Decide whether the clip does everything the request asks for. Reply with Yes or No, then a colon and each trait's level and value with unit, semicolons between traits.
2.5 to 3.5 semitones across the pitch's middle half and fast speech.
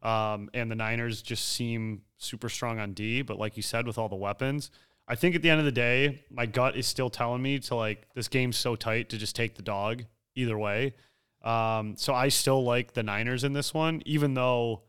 Yes: average, 2.9 semitones; fast, 230 wpm